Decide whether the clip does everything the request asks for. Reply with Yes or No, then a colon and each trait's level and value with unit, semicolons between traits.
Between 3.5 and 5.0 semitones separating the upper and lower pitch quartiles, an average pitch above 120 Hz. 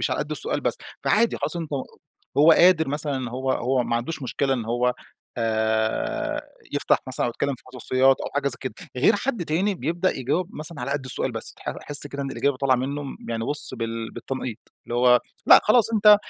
Yes: average, 4.1 semitones; low, 135 Hz